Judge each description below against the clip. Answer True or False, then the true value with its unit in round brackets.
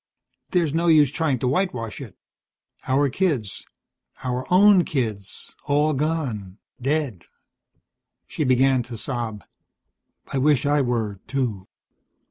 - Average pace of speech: False (115 wpm)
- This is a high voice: False (135 Hz)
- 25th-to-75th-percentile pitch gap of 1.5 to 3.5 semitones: False (4.5 semitones)